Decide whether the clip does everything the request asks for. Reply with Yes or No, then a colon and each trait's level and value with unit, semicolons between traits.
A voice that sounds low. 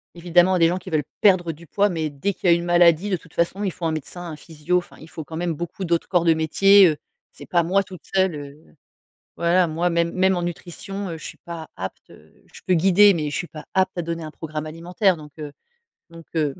No: medium, 170 Hz